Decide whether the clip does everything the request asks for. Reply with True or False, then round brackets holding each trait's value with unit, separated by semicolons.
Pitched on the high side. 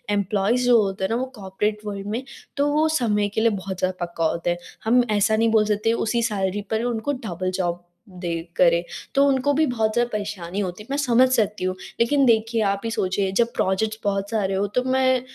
True (210 Hz)